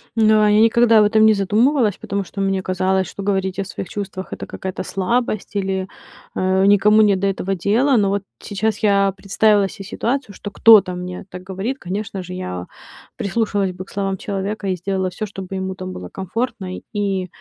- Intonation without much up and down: Yes, narrow, 2.0 semitones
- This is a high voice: Yes, high, 195 Hz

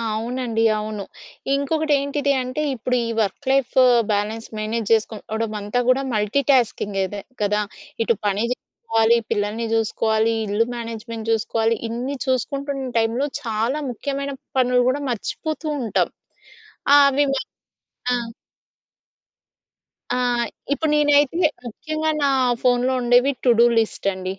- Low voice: No, high, 235 Hz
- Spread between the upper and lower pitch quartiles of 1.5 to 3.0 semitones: No, average, 3.9 semitones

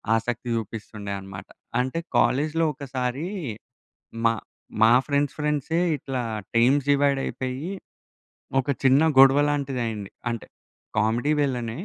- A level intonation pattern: No, average, 3.6 semitones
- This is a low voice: Yes, low, 130 Hz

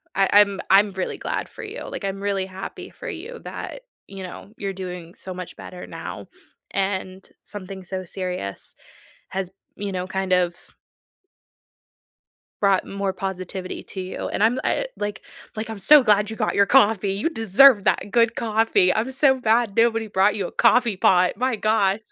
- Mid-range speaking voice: No, high, 200 Hz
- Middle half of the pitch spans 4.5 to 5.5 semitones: No, average, 2.9 semitones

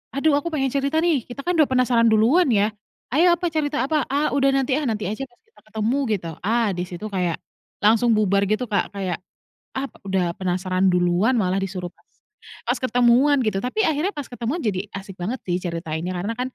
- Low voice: No, high, 225 Hz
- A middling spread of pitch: No, wide, 6.7 semitones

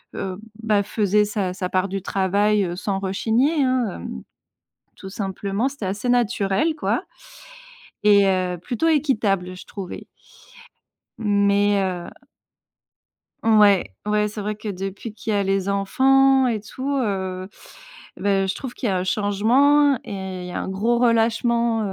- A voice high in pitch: Yes, high, 205 Hz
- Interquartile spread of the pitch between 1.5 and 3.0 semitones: No, average, 3.4 semitones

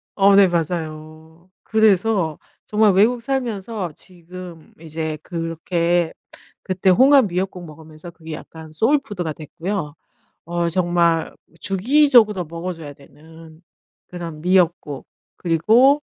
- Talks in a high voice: No, medium, 175 Hz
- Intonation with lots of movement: No, average, 3.7 semitones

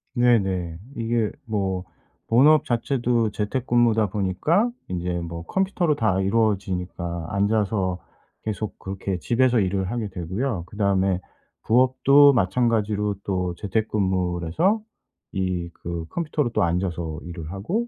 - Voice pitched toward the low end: Yes, low, 100 Hz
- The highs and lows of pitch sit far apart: No, average, 4.6 semitones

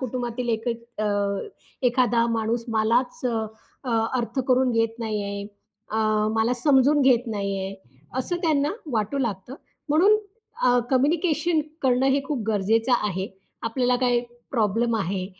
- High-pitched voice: Yes, high, 240 Hz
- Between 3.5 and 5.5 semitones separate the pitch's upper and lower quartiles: No, average, 3.1 semitones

